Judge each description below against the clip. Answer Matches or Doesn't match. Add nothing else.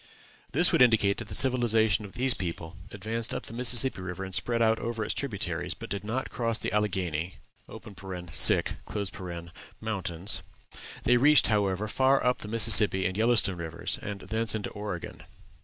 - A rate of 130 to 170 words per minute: Matches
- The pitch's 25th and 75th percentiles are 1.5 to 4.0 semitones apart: Matches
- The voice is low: Matches